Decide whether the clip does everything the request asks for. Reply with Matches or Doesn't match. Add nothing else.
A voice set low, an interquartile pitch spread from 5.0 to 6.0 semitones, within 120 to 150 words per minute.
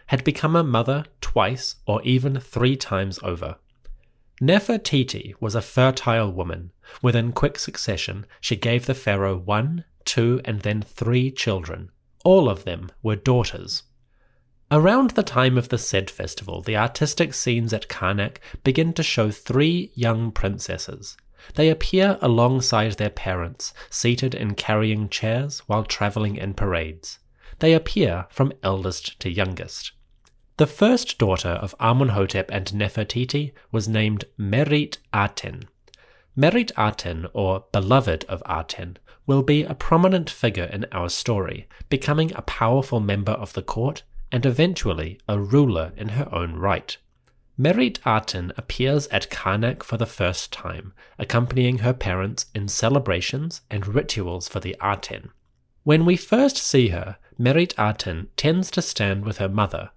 Matches